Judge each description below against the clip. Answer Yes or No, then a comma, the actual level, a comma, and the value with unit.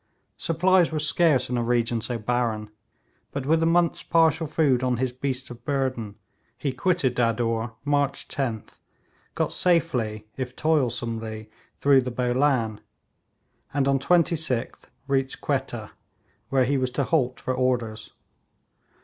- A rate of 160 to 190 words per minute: No, slow, 135 wpm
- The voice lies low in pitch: Yes, low, 130 Hz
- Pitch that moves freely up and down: No, average, 3.7 semitones